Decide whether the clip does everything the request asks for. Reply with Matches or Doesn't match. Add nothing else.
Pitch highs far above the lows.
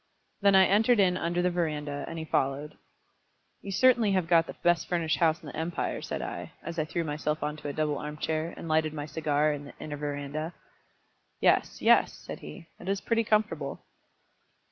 Doesn't match